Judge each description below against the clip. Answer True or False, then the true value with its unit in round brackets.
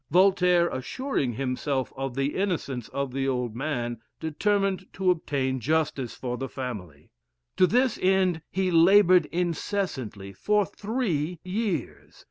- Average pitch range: False (6.3 semitones)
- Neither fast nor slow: False (125 wpm)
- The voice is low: False (160 Hz)